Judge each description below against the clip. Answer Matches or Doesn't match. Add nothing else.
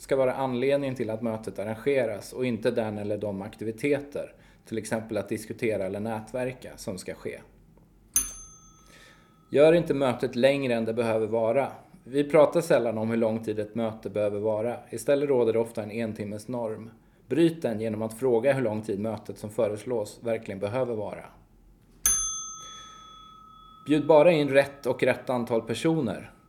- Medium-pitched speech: Doesn't match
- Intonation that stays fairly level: Doesn't match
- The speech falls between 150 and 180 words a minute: Matches